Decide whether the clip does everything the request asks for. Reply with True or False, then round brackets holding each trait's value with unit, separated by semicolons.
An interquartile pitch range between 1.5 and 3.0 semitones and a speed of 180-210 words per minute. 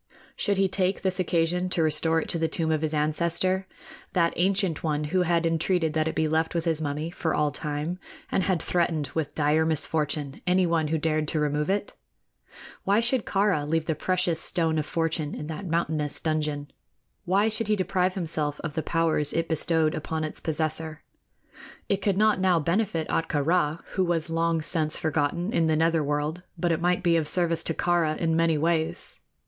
True (2.5 semitones; 195 wpm)